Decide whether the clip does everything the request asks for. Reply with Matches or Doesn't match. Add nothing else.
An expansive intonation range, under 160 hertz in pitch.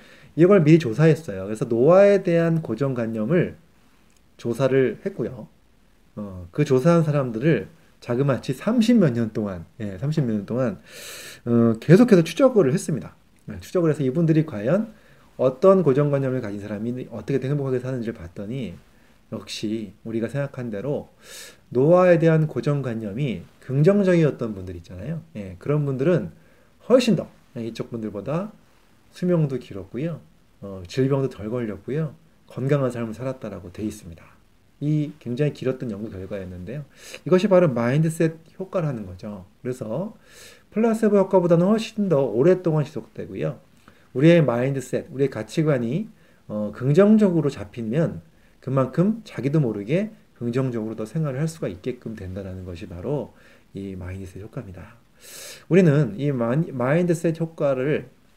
Matches